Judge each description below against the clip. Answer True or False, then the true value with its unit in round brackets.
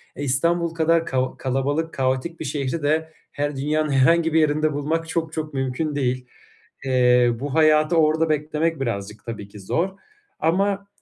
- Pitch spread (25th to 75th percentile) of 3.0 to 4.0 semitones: True (3.6 semitones)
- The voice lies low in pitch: False (150 Hz)